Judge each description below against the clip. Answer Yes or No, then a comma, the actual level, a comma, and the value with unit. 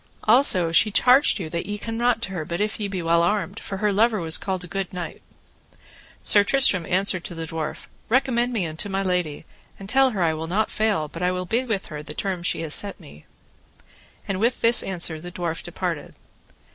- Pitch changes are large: No, average, 4.2 semitones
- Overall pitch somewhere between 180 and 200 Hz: Yes, high, 190 Hz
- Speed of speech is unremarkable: No, fast, 220 wpm